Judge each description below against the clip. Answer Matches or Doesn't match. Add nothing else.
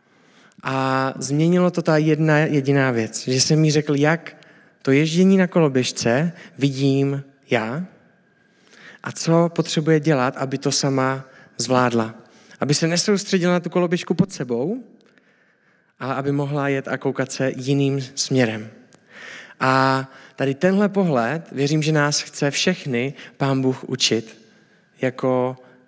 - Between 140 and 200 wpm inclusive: Doesn't match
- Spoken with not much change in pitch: Doesn't match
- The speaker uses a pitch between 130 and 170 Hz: Matches